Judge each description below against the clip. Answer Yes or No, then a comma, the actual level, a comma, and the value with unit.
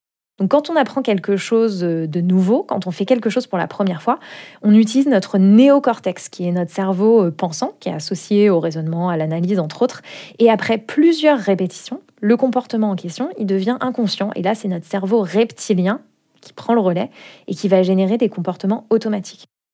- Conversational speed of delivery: Yes, average, 190 wpm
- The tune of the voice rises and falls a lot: No, average, 4.0 semitones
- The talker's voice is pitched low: No, high, 205 Hz